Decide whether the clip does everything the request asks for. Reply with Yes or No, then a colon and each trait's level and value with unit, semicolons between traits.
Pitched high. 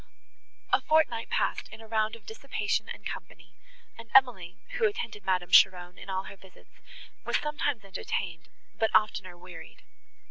Yes: high, 210 Hz